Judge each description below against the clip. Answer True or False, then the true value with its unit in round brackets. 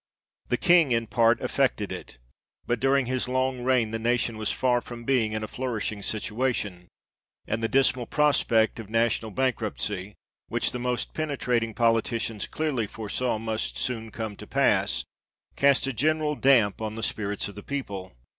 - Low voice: True (115 Hz)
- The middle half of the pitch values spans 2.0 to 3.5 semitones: True (3.0 semitones)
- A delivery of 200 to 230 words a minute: False (165 wpm)